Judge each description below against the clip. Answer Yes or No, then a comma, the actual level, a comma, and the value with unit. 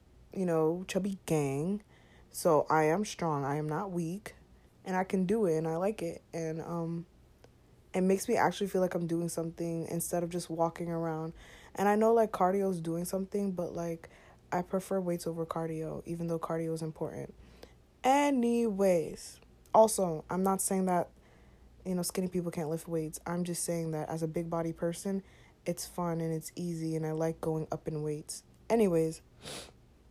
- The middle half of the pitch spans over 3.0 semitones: No, average, 2.7 semitones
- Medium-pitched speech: Yes, medium, 170 Hz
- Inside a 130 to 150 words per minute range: No, average, 185 wpm